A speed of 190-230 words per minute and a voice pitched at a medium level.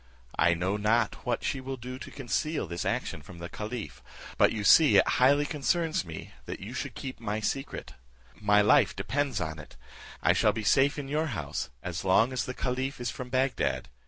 No: average, 200 wpm; low, 120 Hz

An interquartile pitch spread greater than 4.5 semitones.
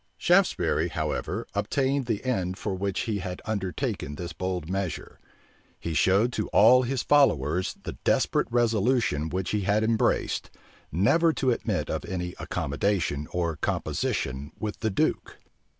Yes: average, 5.0 semitones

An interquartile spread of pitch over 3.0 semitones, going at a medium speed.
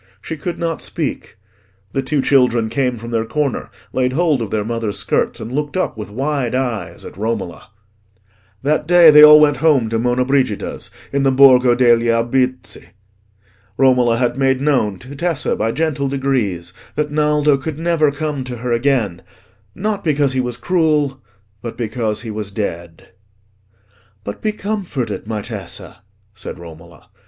Yes: average, 4.6 semitones; average, 160 wpm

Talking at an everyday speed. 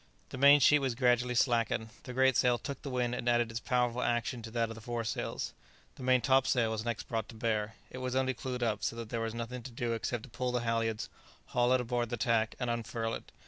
No: fast, 255 wpm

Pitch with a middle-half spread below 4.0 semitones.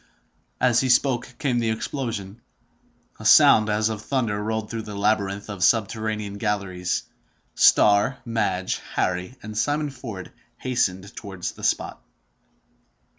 Yes: average, 2.9 semitones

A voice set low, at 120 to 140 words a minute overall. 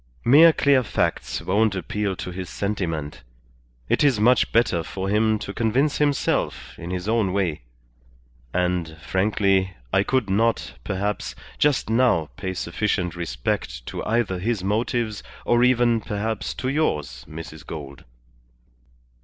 Yes: low, 100 Hz; slow, 135 wpm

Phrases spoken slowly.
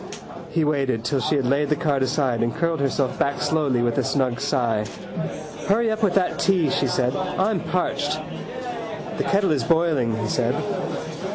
No: average, 175 wpm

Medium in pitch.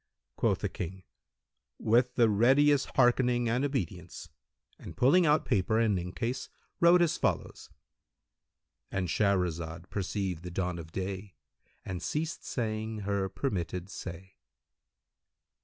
No: low, 105 Hz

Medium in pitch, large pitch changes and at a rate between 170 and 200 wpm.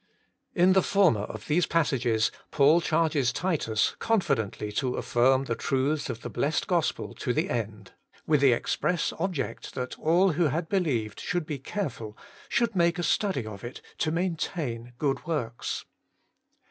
No: medium, 145 Hz; wide, 6.4 semitones; average, 155 wpm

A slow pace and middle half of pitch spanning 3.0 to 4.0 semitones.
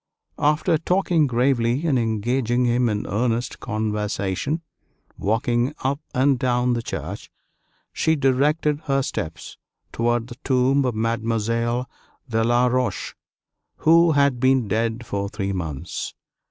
Yes: slow, 125 wpm; average, 3.3 semitones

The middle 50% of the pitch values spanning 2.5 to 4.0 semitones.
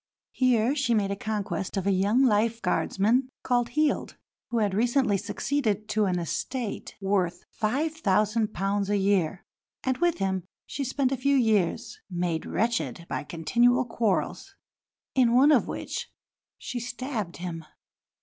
No: average, 4.6 semitones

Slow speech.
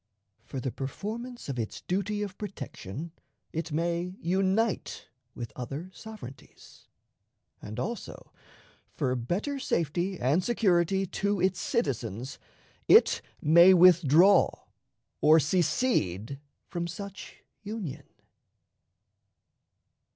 Yes: slow, 95 wpm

